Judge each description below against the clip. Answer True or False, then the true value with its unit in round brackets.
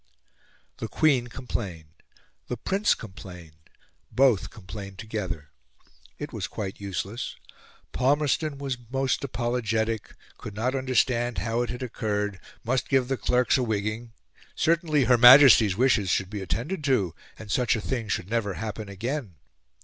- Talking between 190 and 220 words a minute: False (140 wpm)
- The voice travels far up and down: False (4.2 semitones)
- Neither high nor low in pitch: False (115 Hz)